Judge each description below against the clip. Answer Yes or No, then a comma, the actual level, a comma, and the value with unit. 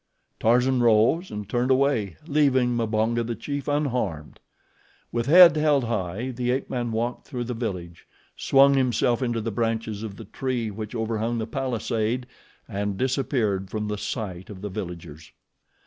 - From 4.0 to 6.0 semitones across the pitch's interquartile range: No, average, 3.4 semitones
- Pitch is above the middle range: No, low, 115 Hz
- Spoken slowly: No, average, 155 wpm